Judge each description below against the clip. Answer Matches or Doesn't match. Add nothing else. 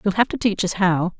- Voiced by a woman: Matches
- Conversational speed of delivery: Doesn't match